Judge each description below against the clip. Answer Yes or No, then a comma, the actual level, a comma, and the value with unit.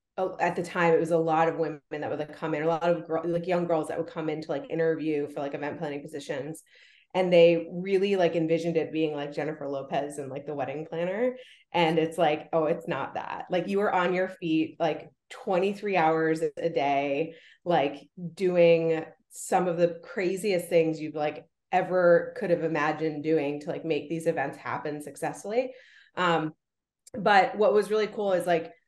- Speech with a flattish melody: Yes, narrow, 2.3 semitones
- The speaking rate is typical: Yes, average, 195 wpm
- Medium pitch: Yes, medium, 165 Hz